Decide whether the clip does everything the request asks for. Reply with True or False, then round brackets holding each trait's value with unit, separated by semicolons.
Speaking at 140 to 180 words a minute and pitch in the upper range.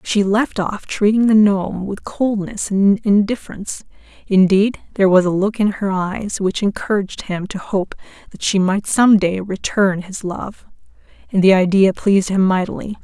True (170 wpm; 200 Hz)